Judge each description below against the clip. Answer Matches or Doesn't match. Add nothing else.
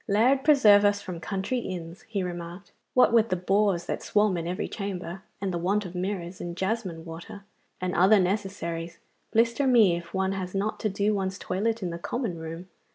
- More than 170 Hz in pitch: Matches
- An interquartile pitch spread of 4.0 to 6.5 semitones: Doesn't match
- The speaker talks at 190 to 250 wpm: Matches